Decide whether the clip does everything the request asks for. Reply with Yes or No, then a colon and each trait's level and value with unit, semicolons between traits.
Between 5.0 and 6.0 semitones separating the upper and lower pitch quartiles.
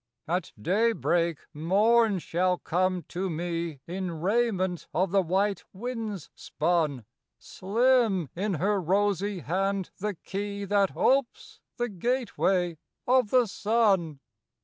No: average, 3.6 semitones